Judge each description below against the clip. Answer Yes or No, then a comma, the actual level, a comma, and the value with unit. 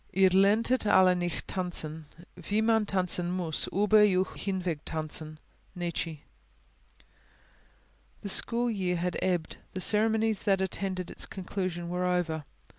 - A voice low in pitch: No, medium, 185 Hz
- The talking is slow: Yes, slow, 125 wpm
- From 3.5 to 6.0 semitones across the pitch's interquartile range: No, narrow, 2.6 semitones